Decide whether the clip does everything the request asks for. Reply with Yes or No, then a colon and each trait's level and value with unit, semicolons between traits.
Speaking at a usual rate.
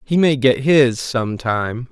Yes: average, 190 wpm